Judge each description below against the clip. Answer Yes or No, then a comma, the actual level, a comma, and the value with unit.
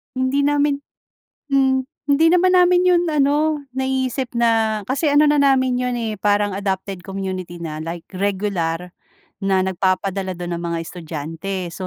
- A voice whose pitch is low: No, high, 205 Hz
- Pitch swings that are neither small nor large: No, wide, 6.9 semitones